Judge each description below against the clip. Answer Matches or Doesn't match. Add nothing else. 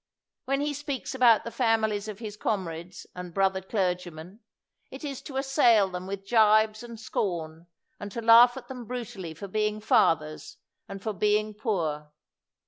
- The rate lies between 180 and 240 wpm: Doesn't match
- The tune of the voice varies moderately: Matches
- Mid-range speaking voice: Doesn't match